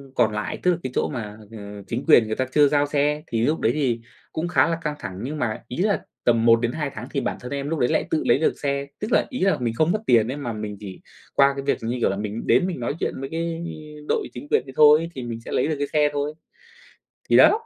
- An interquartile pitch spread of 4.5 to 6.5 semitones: Yes, average, 4.8 semitones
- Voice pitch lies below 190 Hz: Yes, medium, 140 Hz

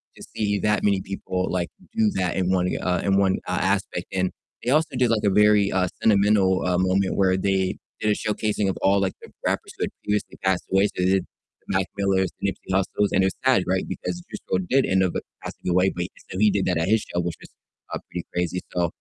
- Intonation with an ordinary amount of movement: No, narrow, 1.9 semitones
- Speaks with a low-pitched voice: Yes, very low, 95 Hz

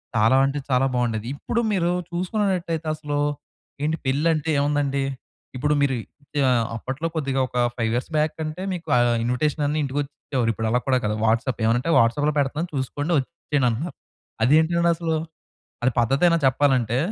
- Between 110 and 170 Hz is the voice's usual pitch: Yes, medium, 140 Hz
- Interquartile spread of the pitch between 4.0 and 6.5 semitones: Yes, average, 4.3 semitones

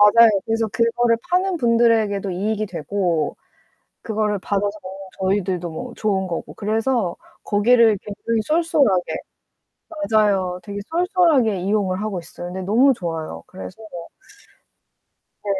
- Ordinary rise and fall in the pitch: Yes, average, 3.6 semitones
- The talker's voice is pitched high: Yes, high, 210 Hz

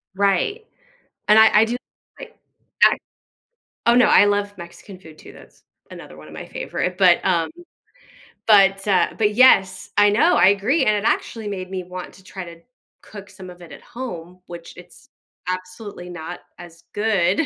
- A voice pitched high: Yes, high, 195 Hz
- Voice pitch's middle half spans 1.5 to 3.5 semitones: Yes, average, 2.9 semitones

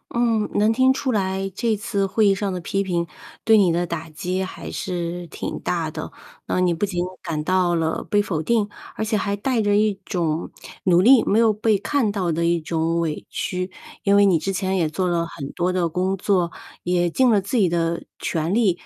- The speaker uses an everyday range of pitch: Yes, average, 3.3 semitones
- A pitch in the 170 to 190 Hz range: Yes, medium, 185 Hz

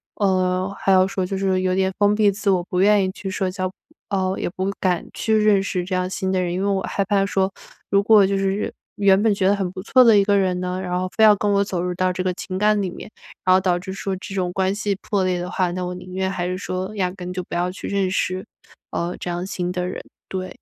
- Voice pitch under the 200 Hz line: Yes, high, 190 Hz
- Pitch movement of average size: No, narrow, 1.4 semitones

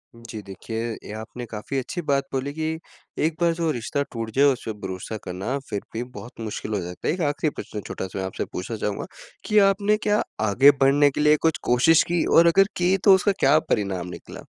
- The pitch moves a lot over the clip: Yes, wide, 7.1 semitones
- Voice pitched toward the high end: No, low, 130 Hz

